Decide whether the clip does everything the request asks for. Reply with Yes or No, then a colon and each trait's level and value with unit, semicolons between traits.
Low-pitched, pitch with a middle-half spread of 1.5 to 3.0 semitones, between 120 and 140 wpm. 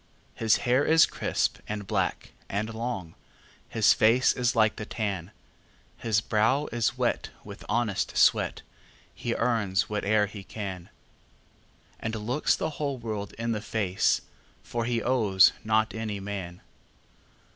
Yes: low, 110 Hz; narrow, 2.5 semitones; slow, 135 wpm